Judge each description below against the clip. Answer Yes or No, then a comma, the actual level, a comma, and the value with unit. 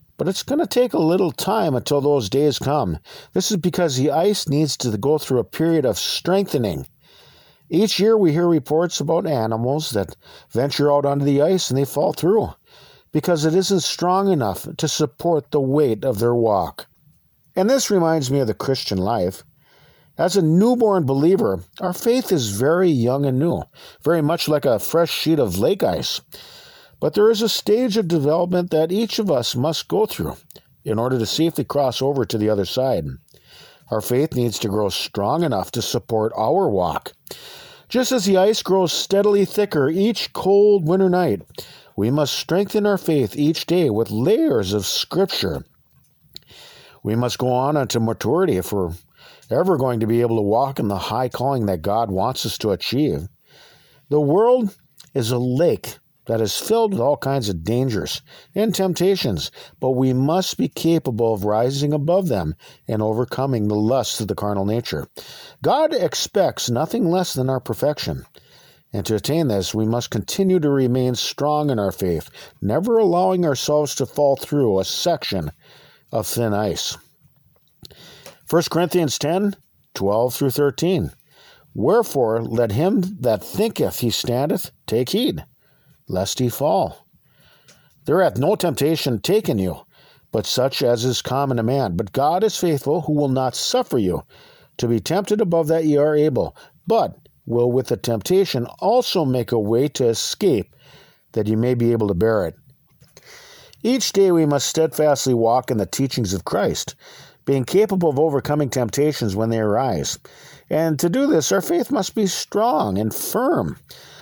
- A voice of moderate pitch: Yes, medium, 145 Hz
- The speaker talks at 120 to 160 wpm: No, average, 170 wpm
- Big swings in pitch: Yes, wide, 7.0 semitones